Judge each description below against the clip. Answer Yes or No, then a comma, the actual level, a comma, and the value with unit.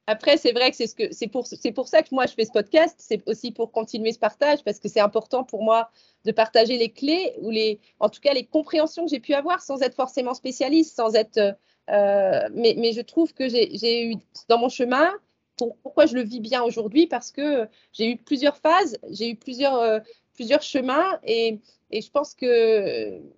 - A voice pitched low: No, very high, 250 Hz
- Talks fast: Yes, fast, 225 wpm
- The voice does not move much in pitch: No, average, 4.5 semitones